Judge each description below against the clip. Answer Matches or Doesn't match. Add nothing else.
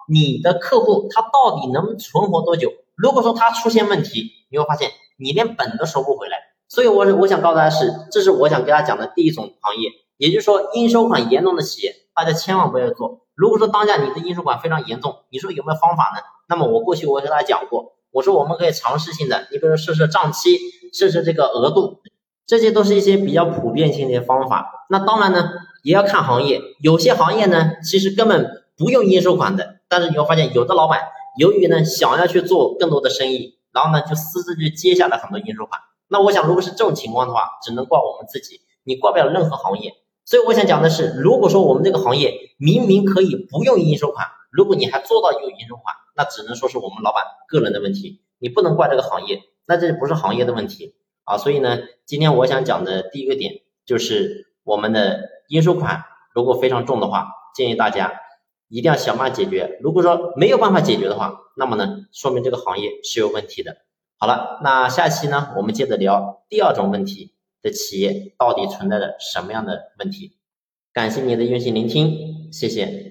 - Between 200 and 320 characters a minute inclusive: Doesn't match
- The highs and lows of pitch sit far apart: Matches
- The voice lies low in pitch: Doesn't match